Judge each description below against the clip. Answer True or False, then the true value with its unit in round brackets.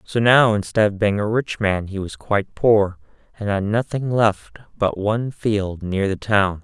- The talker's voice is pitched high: False (105 Hz)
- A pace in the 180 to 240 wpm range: True (200 wpm)